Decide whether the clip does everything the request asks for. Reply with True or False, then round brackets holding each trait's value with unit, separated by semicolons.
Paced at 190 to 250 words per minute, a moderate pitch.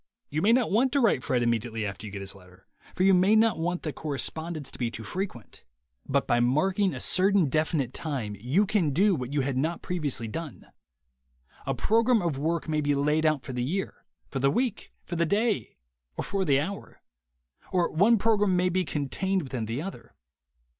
True (200 wpm; 160 Hz)